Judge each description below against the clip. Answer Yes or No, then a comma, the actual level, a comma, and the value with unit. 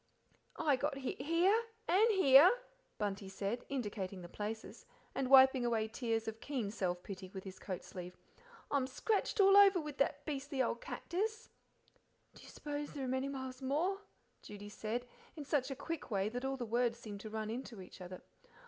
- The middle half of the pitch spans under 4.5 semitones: No, wide, 5.5 semitones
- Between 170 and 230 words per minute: Yes, average, 185 wpm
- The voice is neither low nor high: No, very high, 255 Hz